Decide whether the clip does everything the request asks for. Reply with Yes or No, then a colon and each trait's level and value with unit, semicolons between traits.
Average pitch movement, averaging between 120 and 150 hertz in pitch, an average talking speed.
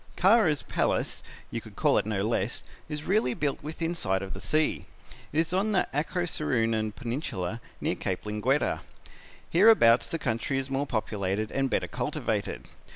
No: wide, 6.7 semitones; low, 135 Hz; average, 155 wpm